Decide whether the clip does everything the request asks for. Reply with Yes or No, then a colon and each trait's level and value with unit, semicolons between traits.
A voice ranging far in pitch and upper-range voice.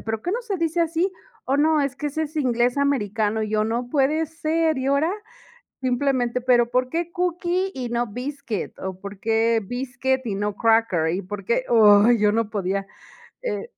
Yes: wide, 5.8 semitones; very high, 250 Hz